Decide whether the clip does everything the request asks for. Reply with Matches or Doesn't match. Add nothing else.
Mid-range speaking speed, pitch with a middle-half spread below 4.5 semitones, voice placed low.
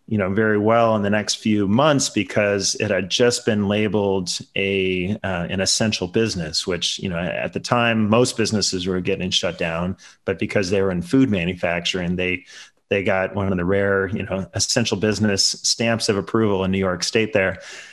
Matches